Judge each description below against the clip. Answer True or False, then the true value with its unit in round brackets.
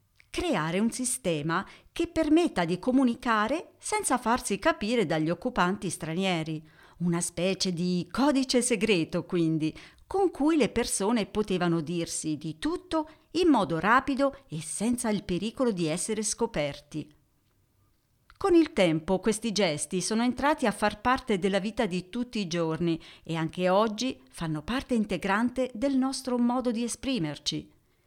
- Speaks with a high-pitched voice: True (210 Hz)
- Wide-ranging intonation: True (7.0 semitones)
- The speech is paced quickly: False (135 wpm)